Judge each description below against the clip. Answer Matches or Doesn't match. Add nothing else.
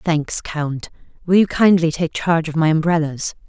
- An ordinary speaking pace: Matches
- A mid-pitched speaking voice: Matches